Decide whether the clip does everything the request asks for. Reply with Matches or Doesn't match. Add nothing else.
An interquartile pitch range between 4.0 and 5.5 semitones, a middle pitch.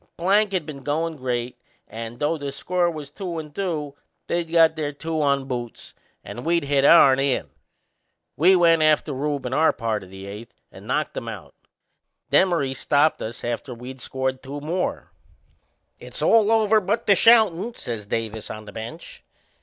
Matches